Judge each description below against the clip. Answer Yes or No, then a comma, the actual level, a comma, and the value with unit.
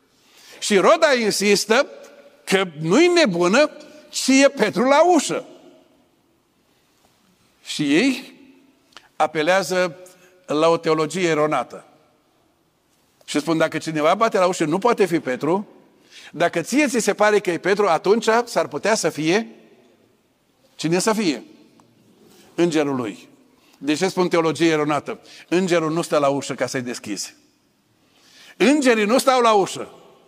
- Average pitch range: No, wide, 8.4 semitones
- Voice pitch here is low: No, high, 190 Hz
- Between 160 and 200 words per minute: No, average, 130 wpm